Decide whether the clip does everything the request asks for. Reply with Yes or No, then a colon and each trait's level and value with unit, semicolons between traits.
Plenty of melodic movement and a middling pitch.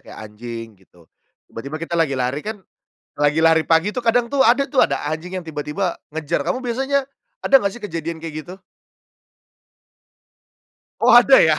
Yes: wide, 7.6 semitones; medium, 165 Hz